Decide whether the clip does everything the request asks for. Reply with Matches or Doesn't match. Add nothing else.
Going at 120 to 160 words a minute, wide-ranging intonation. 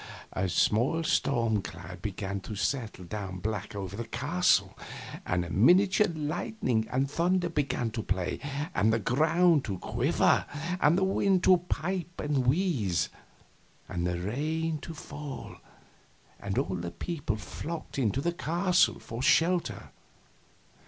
Matches